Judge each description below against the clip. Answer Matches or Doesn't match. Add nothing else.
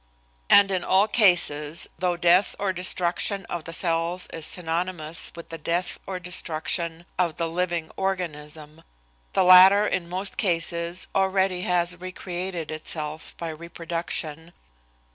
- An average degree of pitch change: Doesn't match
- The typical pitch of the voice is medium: Matches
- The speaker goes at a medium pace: Doesn't match